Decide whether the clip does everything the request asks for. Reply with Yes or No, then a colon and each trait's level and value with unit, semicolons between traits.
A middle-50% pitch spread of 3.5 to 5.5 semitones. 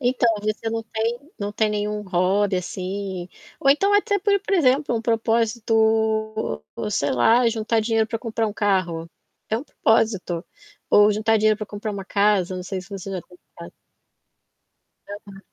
No: narrow, 2.6 semitones